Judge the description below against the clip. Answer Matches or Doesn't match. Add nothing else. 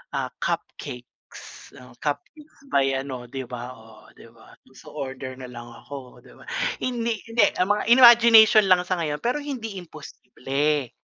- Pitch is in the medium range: Matches